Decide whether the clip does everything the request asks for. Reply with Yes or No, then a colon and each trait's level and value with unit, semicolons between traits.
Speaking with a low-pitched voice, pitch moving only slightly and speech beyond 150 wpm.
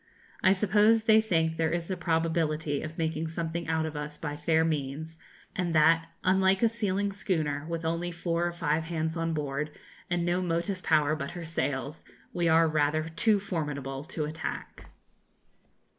No: medium, 165 Hz; narrow, 2.1 semitones; average, 170 wpm